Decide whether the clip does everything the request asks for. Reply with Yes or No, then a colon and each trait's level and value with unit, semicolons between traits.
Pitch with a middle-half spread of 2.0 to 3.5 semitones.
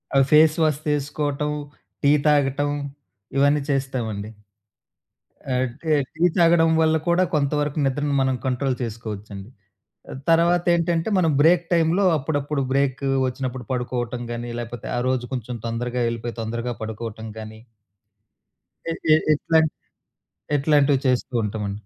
No: average, 4.1 semitones